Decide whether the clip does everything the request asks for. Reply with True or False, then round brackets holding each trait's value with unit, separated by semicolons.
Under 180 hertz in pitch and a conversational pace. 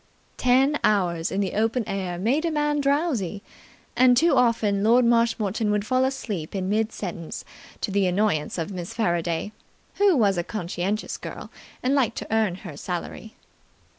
False (215 Hz; 165 wpm)